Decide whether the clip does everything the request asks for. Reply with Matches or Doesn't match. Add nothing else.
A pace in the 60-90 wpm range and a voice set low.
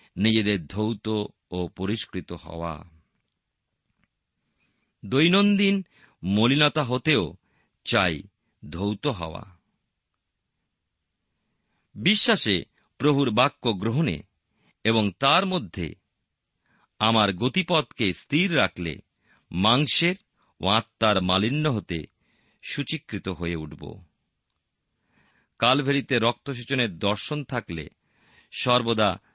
Matches